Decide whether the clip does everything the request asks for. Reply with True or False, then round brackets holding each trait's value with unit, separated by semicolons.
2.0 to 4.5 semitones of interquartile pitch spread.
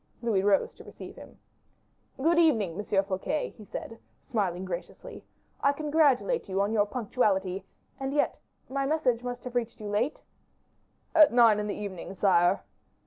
False (5.6 semitones)